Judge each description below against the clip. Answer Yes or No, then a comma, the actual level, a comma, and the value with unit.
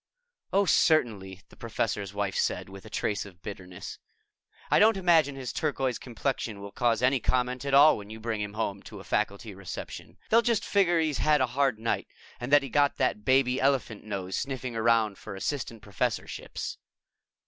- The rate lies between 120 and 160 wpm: No, average, 180 wpm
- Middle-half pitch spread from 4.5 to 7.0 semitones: Yes, average, 5.3 semitones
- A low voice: Yes, low, 120 Hz